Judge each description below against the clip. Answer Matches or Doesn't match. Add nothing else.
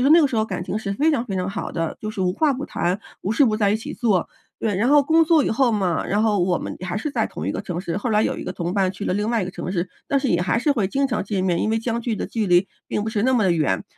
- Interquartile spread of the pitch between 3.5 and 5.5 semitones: Matches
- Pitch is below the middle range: Doesn't match